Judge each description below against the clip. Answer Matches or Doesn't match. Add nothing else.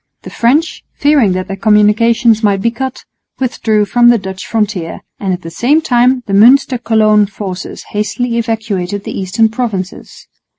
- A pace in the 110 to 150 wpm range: Doesn't match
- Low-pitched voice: Doesn't match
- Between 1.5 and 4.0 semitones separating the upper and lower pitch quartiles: Matches